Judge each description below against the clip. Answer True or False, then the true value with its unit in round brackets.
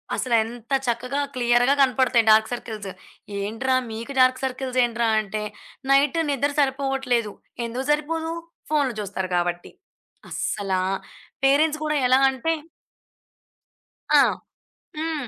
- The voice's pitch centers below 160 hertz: False (255 Hz)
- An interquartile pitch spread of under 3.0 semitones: False (3.4 semitones)